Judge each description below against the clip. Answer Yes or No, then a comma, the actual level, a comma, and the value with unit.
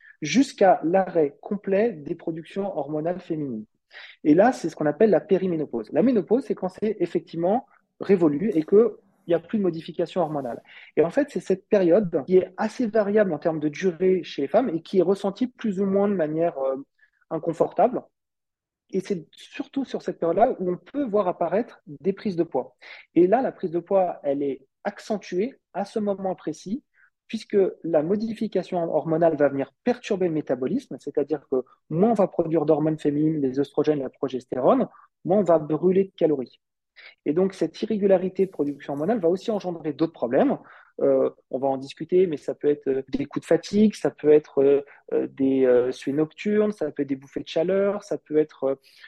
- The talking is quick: No, average, 195 wpm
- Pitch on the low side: No, medium, 175 Hz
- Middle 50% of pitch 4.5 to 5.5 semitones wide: Yes, average, 4.9 semitones